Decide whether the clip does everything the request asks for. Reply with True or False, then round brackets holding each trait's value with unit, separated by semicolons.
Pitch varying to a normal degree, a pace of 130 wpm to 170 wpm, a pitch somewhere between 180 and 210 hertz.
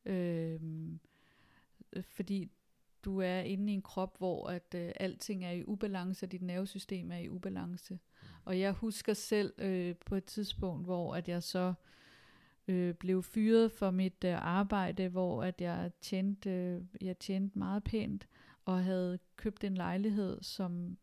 False (1.9 semitones; 155 wpm; 185 Hz)